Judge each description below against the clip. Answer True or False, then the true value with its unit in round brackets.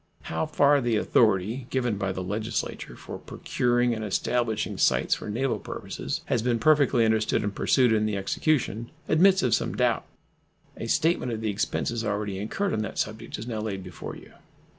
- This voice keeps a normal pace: True (180 wpm)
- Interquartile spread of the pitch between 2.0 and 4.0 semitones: True (3.0 semitones)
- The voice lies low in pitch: True (115 Hz)